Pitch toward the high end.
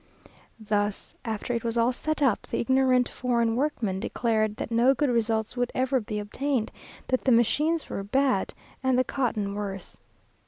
Yes: high, 235 Hz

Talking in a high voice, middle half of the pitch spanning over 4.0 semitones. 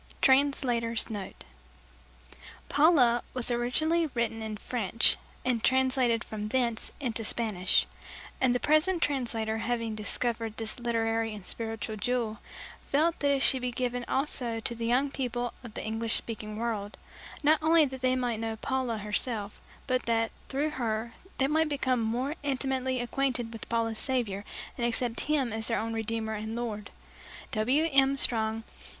No: high, 235 Hz; average, 2.9 semitones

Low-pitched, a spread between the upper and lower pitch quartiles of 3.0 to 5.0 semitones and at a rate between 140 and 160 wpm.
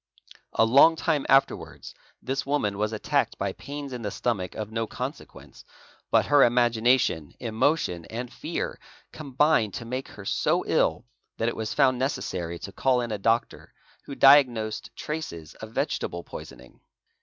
Yes: low, 120 Hz; average, 4.2 semitones; average, 155 wpm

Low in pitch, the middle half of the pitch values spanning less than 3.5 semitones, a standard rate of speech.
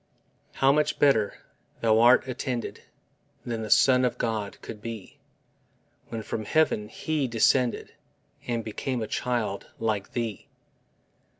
No: low, 115 Hz; average, 2.8 semitones; slow, 120 wpm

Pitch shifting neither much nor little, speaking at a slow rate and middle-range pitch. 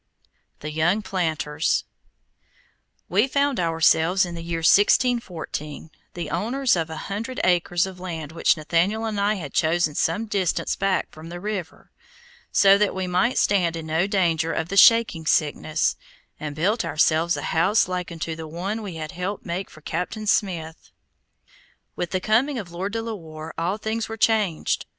No: average, 4.1 semitones; average, 170 wpm; medium, 180 Hz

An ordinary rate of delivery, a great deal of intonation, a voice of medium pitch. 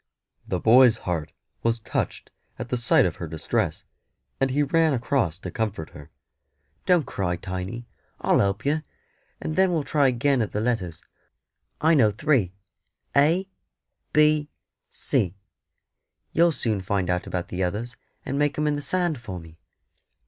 No: average, 155 wpm; wide, 7.9 semitones; low, 120 Hz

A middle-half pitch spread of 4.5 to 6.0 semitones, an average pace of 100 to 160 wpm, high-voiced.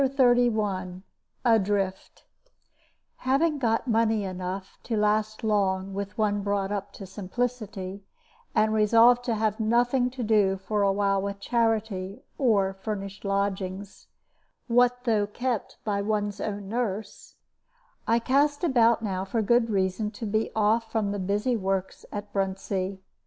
No: average, 2.8 semitones; average, 140 wpm; high, 210 Hz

